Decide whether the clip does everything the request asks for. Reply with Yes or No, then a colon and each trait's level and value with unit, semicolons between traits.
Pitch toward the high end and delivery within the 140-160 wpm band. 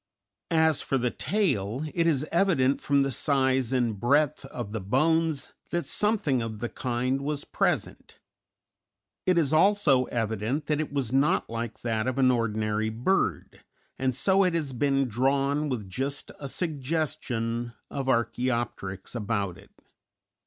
No: low, 130 Hz; average, 145 wpm